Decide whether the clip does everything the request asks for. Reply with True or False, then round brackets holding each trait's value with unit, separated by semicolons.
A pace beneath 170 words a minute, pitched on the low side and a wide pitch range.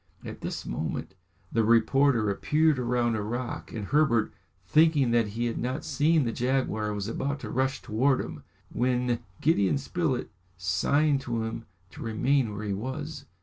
False (160 wpm; 125 Hz; 4.0 semitones)